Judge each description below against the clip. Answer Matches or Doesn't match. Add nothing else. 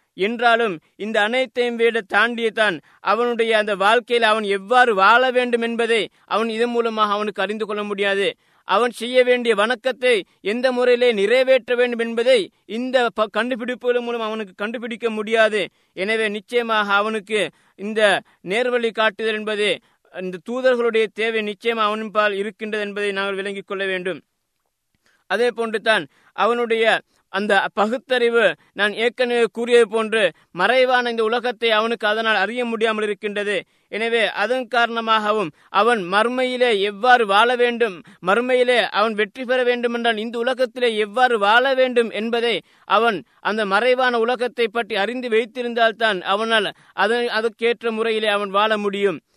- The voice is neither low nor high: Doesn't match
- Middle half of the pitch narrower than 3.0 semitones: Matches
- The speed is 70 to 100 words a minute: Doesn't match